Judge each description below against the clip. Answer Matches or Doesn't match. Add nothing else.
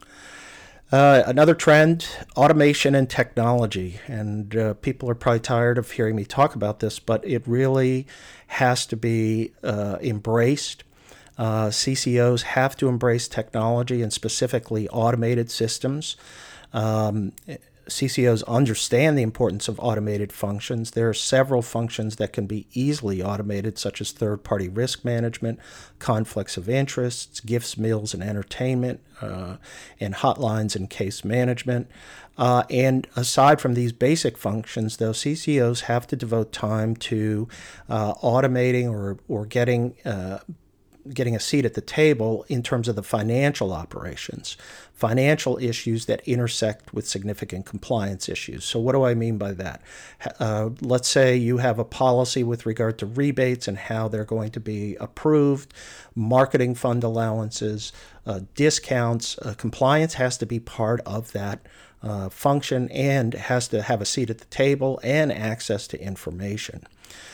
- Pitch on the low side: Matches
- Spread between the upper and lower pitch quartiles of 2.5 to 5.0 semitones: Matches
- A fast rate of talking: Doesn't match